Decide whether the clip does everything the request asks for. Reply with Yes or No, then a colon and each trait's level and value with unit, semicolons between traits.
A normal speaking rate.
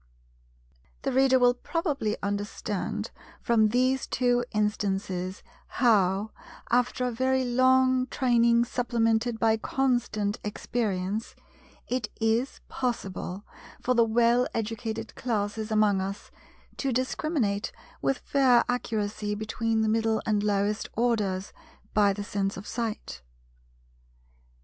No: slow, 105 wpm